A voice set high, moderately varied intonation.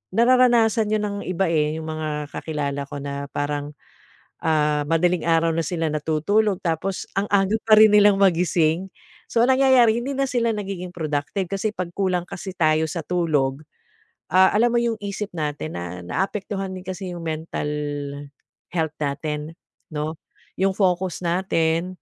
No: medium, 175 Hz; average, 4.5 semitones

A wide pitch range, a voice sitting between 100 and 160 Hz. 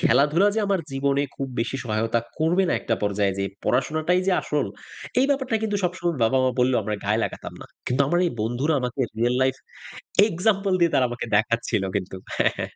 Yes: wide, 6.9 semitones; low, 135 Hz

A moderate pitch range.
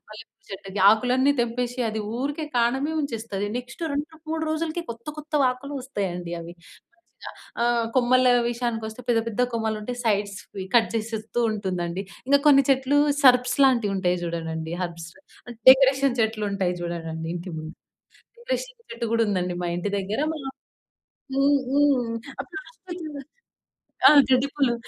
No: wide, 5.7 semitones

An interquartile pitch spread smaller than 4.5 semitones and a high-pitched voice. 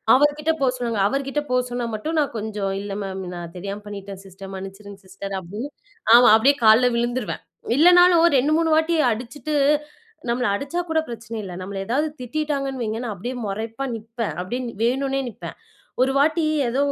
No: wide, 5.5 semitones; high, 240 Hz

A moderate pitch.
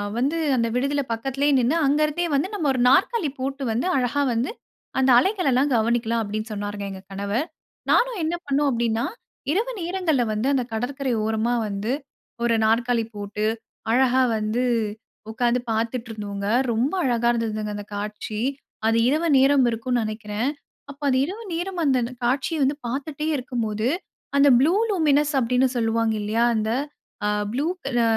No: high, 245 Hz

